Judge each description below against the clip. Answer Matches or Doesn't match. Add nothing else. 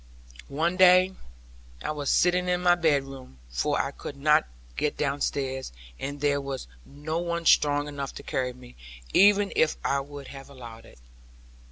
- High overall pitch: Doesn't match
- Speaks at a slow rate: Doesn't match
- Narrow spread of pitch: Doesn't match